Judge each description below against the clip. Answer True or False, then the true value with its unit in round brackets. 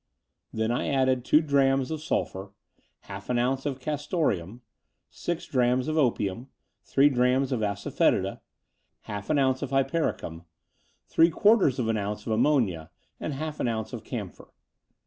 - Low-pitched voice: True (130 Hz)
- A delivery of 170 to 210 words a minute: False (150 wpm)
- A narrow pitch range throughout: False (4.4 semitones)